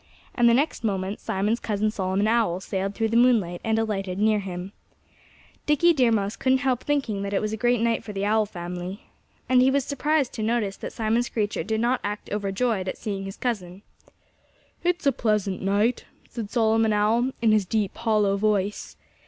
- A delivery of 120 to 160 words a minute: No, average, 190 wpm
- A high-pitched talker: Yes, high, 215 Hz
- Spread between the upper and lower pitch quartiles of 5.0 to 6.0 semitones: No, average, 3.1 semitones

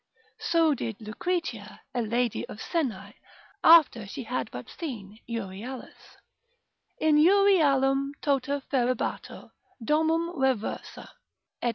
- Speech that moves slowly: Yes, slow, 100 wpm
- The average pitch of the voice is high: Yes, very high, 265 Hz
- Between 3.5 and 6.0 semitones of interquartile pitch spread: Yes, wide, 5.5 semitones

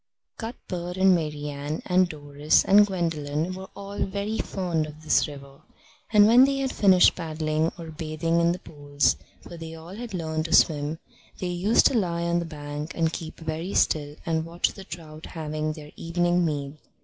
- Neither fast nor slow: Yes, average, 180 wpm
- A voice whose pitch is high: No, medium, 165 Hz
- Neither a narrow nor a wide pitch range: Yes, average, 3.1 semitones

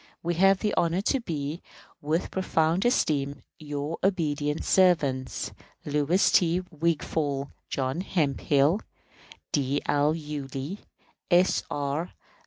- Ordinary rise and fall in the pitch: Yes, average, 3.8 semitones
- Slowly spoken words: Yes, slow, 105 wpm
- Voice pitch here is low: No, medium, 155 Hz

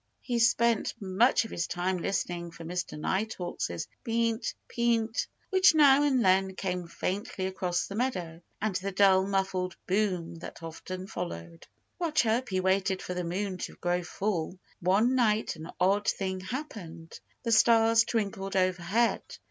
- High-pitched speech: Yes, high, 195 Hz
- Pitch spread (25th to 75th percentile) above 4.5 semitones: No, average, 4.0 semitones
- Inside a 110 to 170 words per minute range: Yes, average, 150 wpm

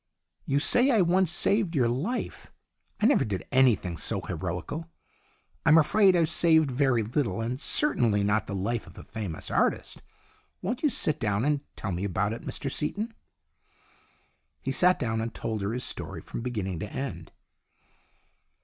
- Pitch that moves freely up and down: Yes, wide, 8.1 semitones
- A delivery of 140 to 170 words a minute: Yes, average, 165 wpm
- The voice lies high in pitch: No, low, 125 Hz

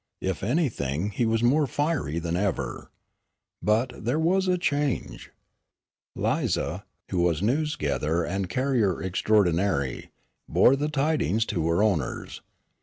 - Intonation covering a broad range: Yes, wide, 8.6 semitones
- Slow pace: Yes, slow, 125 wpm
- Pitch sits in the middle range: No, low, 105 Hz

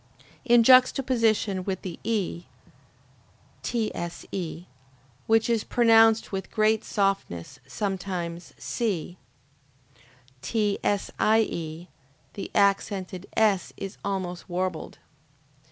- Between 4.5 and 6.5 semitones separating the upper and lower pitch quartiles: No, average, 3.7 semitones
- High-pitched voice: Yes, high, 200 Hz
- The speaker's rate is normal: No, slow, 80 wpm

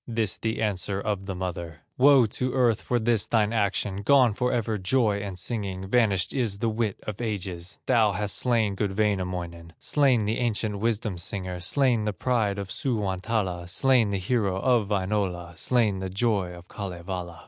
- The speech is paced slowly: No, average, 170 wpm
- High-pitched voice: No, low, 105 Hz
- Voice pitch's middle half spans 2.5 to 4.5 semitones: Yes, average, 3.6 semitones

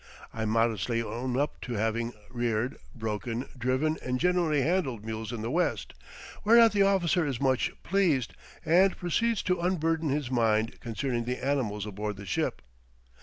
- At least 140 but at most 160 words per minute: Yes, average, 155 wpm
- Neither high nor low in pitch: No, low, 130 Hz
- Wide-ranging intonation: Yes, wide, 6.5 semitones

